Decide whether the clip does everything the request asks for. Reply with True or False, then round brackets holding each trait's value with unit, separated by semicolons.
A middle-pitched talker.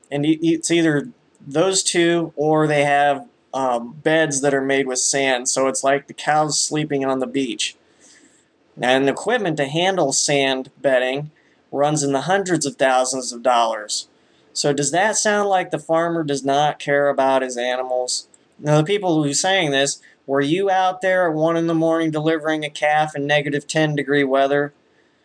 True (145 Hz)